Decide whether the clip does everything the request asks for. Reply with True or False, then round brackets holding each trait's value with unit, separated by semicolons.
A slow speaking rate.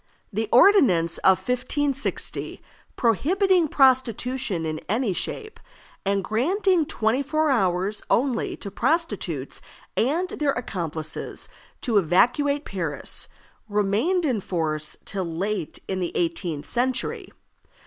True (105 wpm)